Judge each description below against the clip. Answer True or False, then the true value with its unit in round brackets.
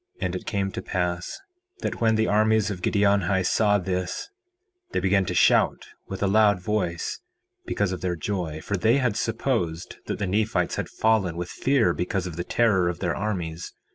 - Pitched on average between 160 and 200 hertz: False (95 Hz)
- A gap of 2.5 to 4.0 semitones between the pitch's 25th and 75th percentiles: True (3.3 semitones)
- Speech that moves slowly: False (190 wpm)